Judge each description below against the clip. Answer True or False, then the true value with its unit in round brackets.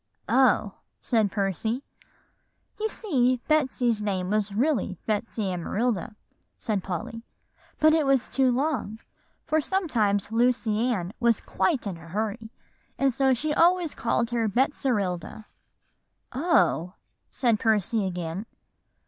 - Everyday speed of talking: False (120 wpm)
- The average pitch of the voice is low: False (230 Hz)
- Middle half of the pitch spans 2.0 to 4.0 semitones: False (4.7 semitones)